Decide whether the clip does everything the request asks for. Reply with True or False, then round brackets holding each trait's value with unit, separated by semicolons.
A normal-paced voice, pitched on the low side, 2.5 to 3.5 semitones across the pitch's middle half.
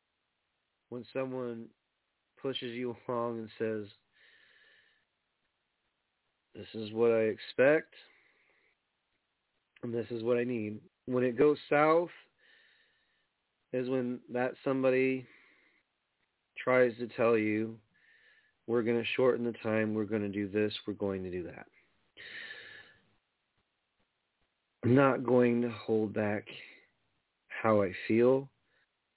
False (115 wpm; 120 Hz; 3.2 semitones)